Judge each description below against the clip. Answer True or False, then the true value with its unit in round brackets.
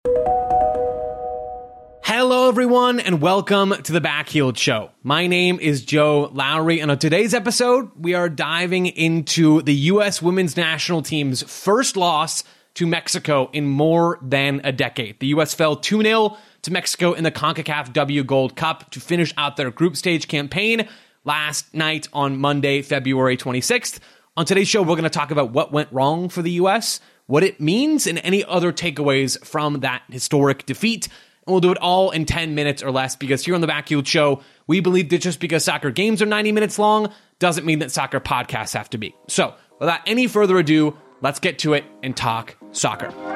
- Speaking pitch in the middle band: True (160 Hz)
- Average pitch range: True (4.4 semitones)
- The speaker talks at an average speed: True (180 wpm)